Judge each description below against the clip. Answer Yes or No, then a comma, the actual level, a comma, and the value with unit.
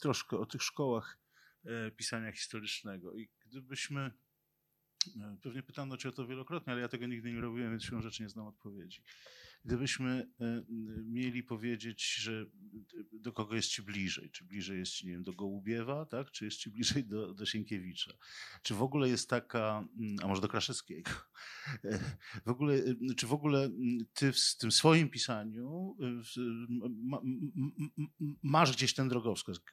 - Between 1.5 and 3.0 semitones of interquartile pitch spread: No, average, 3.5 semitones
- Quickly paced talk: No, average, 145 wpm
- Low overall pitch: Yes, low, 120 Hz